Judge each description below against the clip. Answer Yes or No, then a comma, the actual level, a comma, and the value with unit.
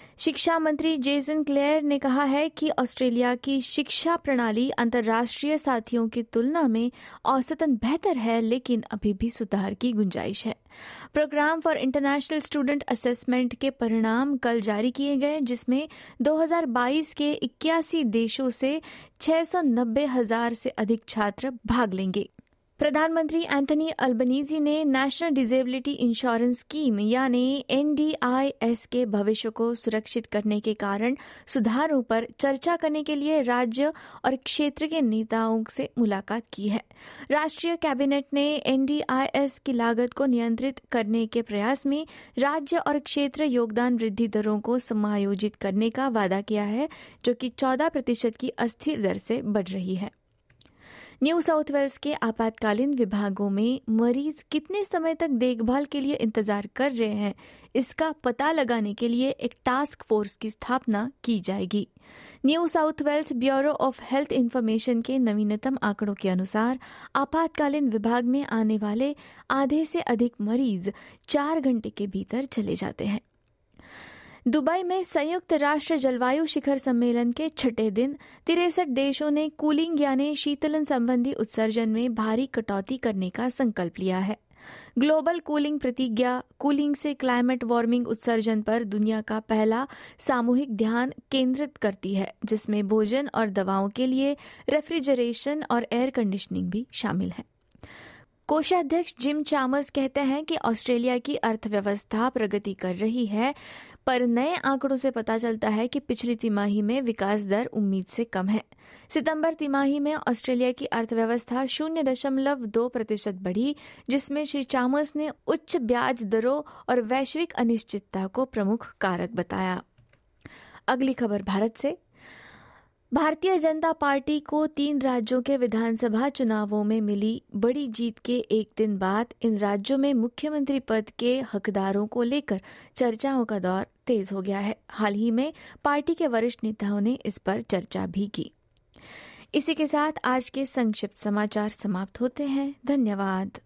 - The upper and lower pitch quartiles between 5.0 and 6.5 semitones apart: No, average, 4.3 semitones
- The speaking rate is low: No, average, 145 wpm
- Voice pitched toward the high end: Yes, very high, 250 Hz